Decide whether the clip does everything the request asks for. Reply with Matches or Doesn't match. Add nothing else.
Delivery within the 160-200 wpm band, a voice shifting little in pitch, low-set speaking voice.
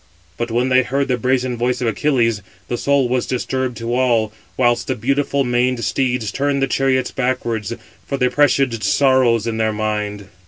Matches